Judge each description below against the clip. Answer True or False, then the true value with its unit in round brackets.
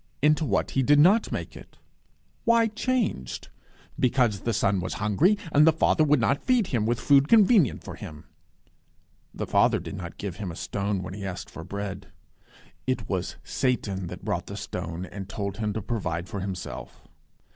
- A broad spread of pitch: True (7.6 semitones)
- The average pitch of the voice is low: True (110 Hz)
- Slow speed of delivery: False (180 wpm)